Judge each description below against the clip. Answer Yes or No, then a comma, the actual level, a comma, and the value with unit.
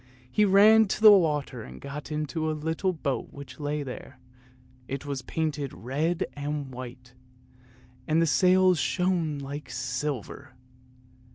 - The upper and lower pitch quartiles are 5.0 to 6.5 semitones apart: No, average, 3.6 semitones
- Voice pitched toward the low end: No, medium, 150 Hz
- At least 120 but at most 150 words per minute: Yes, average, 140 wpm